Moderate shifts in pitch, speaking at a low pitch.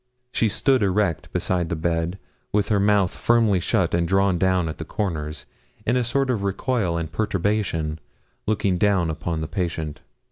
Yes: average, 3.9 semitones; very low, 95 Hz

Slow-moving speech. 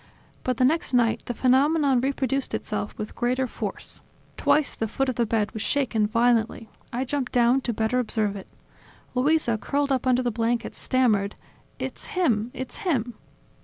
No: average, 165 wpm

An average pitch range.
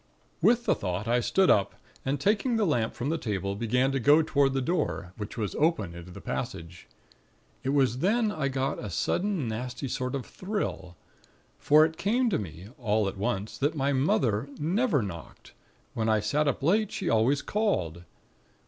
No: wide, 7.2 semitones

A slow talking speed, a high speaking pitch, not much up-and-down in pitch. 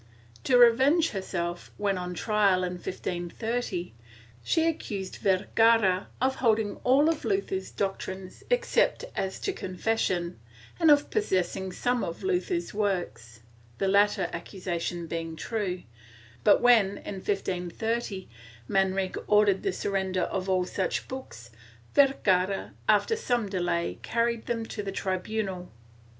No: slow, 130 wpm; high, 195 Hz; average, 4.4 semitones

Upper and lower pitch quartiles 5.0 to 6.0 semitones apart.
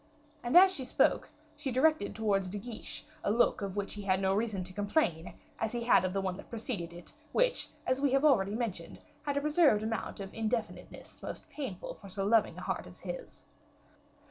Yes: average, 5.3 semitones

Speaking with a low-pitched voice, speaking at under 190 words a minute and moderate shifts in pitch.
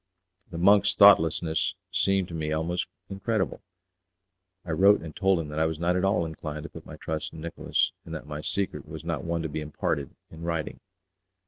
No: very low, 85 Hz; average, 200 wpm; average, 3.5 semitones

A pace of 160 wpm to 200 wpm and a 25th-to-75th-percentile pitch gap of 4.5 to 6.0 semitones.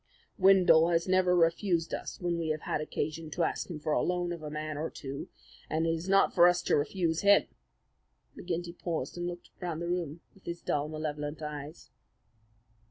No: average, 190 wpm; narrow, 2.4 semitones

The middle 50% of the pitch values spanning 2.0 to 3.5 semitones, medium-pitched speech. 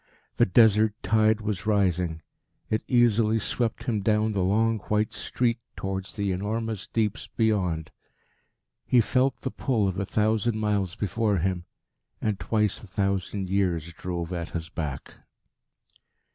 No: average, 2.9 semitones; low, 105 Hz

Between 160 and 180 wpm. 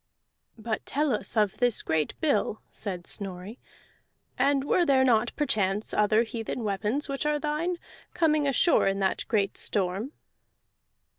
No: average, 140 wpm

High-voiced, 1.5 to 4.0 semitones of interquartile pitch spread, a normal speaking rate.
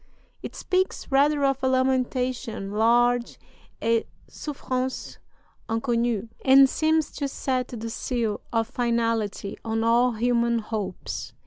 No: high, 240 Hz; narrow, 2.5 semitones; slow, 115 wpm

